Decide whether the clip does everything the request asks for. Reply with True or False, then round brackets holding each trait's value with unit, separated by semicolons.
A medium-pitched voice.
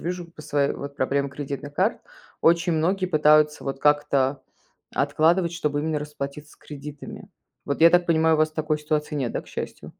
True (150 Hz)